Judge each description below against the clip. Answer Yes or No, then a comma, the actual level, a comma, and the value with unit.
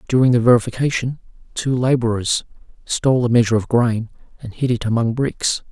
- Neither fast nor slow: Yes, average, 160 wpm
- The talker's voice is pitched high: No, low, 120 Hz